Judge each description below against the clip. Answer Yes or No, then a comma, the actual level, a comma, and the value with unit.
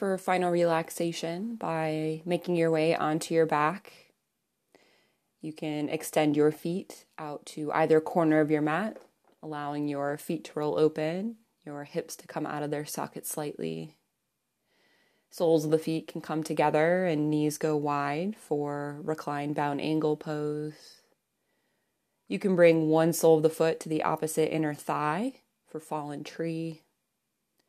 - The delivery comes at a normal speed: Yes, average, 150 wpm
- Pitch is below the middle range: No, medium, 155 Hz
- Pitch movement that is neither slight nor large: No, narrow, 1.6 semitones